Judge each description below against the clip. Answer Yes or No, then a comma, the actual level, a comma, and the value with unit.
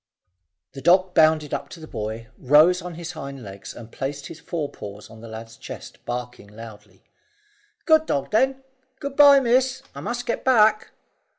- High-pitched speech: No, medium, 150 Hz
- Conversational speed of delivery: Yes, average, 170 wpm